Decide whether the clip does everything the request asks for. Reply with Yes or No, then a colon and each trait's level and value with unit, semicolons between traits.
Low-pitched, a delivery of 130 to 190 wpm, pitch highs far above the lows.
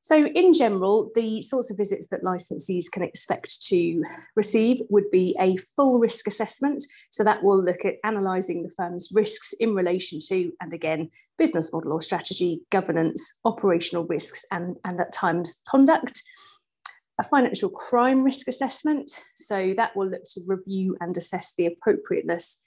No: high, 200 Hz; average, 160 wpm; wide, 6.7 semitones